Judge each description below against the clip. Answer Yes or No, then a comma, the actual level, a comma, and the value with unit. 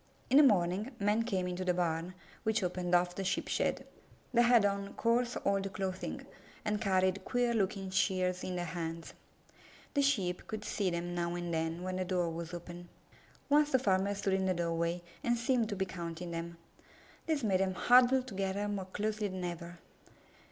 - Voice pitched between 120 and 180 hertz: No, high, 190 Hz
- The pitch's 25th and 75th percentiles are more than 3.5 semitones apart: No, average, 3.2 semitones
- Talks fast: No, average, 185 wpm